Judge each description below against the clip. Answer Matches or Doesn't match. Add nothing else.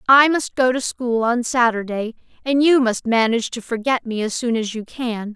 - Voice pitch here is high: Matches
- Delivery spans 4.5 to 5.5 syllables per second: Matches